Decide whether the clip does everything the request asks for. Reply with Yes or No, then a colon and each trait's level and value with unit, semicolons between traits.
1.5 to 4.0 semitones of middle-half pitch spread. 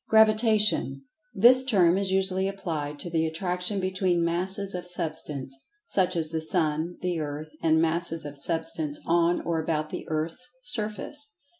Yes: average, 3.3 semitones